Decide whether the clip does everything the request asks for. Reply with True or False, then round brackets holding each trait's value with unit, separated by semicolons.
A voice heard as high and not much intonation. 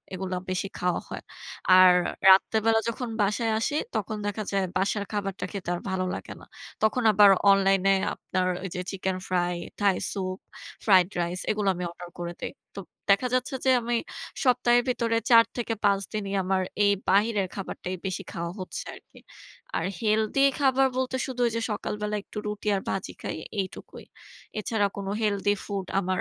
False (200 Hz; 3.0 semitones)